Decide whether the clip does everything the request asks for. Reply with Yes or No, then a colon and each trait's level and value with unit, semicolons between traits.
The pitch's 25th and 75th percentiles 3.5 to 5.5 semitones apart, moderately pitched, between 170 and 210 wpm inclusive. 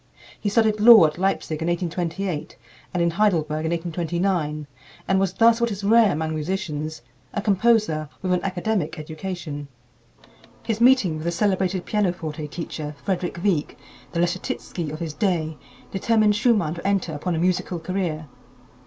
No: average, 3.9 semitones; medium, 175 Hz; average, 155 wpm